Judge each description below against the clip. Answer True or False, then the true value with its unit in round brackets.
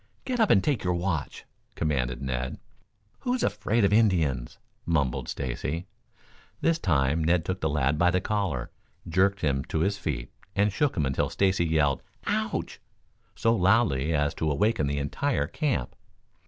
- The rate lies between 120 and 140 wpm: False (155 wpm)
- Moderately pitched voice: False (85 Hz)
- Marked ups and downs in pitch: True (6.1 semitones)